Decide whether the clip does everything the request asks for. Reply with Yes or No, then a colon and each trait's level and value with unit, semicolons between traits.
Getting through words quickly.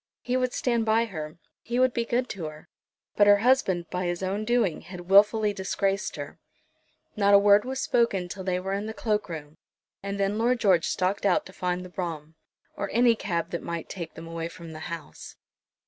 Yes: fast, 210 wpm